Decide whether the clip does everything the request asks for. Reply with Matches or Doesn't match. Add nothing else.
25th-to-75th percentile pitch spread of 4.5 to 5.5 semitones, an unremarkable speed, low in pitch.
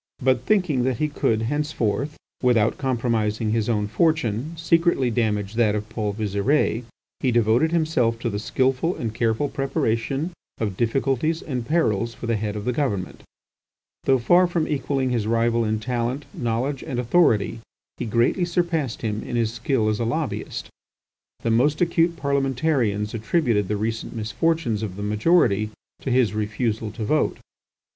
Matches